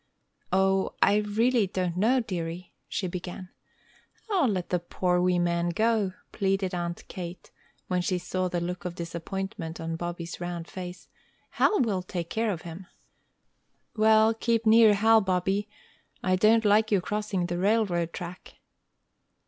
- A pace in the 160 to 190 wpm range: No, average, 150 wpm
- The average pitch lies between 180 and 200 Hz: Yes, medium, 185 Hz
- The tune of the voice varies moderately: Yes, average, 3.3 semitones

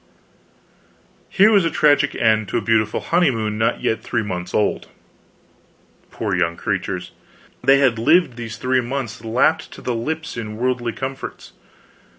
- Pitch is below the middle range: Yes, low, 120 Hz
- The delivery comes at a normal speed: Yes, average, 150 wpm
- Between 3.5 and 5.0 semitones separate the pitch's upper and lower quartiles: Yes, average, 3.8 semitones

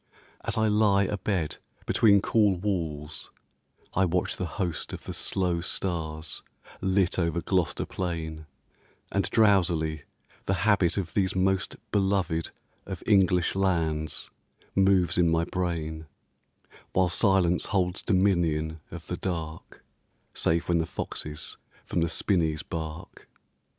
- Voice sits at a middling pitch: No, very low, 90 Hz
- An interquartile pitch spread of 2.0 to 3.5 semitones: Yes, average, 2.9 semitones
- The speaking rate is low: Yes, slow, 125 wpm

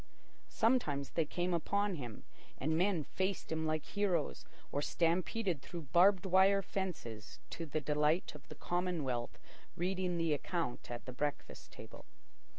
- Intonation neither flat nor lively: Yes, average, 4.1 semitones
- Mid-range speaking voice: Yes, medium, 170 Hz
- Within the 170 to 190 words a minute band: No, average, 145 wpm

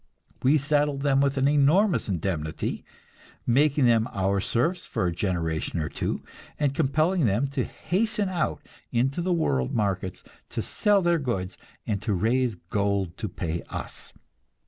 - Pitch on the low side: Yes, low, 125 Hz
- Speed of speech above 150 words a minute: No, average, 145 wpm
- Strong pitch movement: Yes, wide, 7.8 semitones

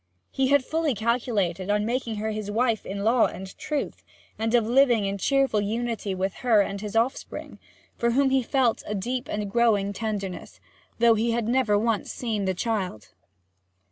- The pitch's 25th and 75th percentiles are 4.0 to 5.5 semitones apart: No, average, 3.1 semitones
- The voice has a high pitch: Yes, high, 225 Hz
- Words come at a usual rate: Yes, average, 175 wpm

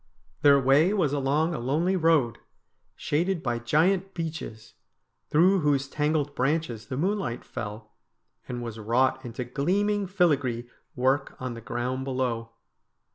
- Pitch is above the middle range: No, medium, 140 Hz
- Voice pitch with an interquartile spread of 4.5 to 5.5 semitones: Yes, average, 5.2 semitones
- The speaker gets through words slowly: Yes, slow, 130 wpm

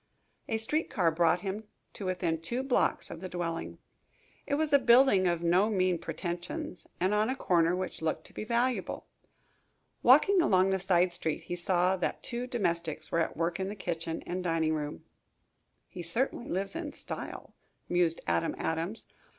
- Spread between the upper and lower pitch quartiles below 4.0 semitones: No, average, 4.5 semitones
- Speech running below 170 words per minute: No, average, 175 wpm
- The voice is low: No, medium, 185 Hz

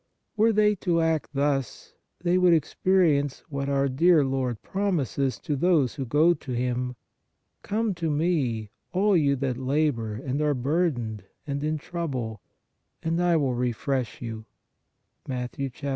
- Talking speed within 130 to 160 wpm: Yes, average, 155 wpm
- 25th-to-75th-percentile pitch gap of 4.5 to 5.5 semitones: Yes, average, 5.0 semitones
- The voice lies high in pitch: No, medium, 140 Hz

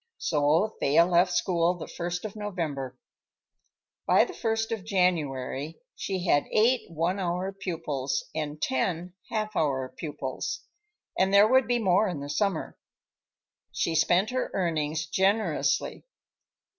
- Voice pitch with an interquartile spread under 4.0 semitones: No, average, 4.5 semitones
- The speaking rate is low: Yes, slow, 130 wpm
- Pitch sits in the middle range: Yes, medium, 175 Hz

